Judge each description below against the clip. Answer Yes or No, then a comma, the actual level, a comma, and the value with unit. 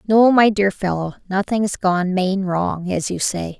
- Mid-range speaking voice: No, high, 195 Hz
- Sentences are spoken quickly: No, average, 185 wpm